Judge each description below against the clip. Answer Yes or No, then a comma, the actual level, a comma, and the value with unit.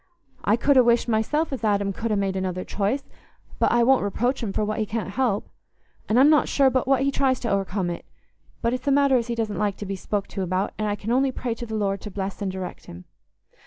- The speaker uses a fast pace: Yes, fast, 260 wpm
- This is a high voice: Yes, high, 220 Hz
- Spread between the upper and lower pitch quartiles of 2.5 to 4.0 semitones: No, average, 4.4 semitones